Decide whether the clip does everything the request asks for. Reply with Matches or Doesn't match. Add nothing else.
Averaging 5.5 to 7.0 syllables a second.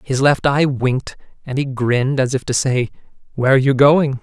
Matches